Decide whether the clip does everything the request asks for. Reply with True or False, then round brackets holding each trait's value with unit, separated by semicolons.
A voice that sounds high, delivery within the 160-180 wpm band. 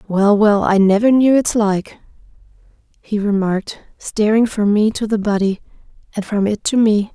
True (210 Hz; 170 wpm)